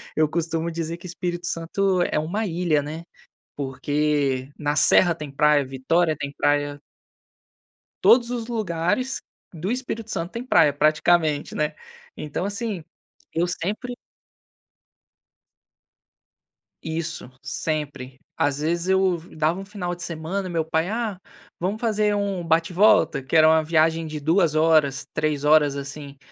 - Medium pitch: Yes, medium, 165 Hz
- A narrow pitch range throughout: No, average, 3.4 semitones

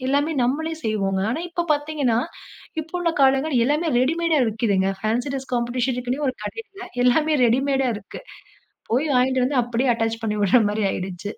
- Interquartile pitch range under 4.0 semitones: No, average, 4.8 semitones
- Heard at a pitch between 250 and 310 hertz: Yes, very high, 255 Hz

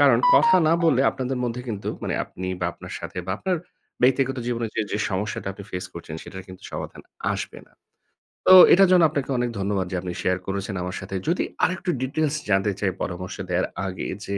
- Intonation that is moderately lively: No, wide, 6.1 semitones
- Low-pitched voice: Yes, low, 100 Hz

